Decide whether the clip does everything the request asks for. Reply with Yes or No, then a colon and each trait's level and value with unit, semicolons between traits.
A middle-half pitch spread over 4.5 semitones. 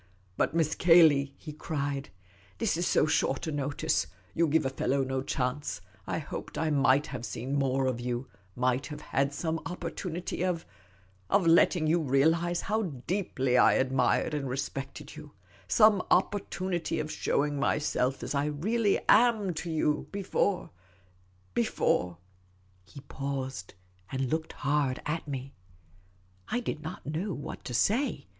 No: average, 4.1 semitones